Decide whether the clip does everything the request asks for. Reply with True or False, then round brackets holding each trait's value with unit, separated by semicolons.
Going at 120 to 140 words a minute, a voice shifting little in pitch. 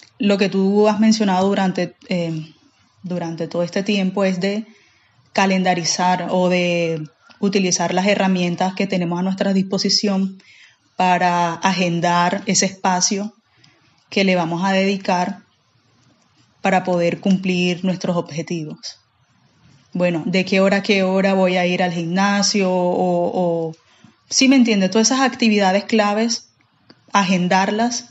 True (130 wpm; 2.2 semitones)